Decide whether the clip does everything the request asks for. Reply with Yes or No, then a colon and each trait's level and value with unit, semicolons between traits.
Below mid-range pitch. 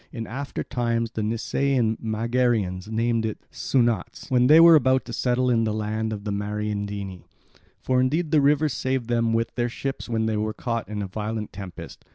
Yes: low, 115 Hz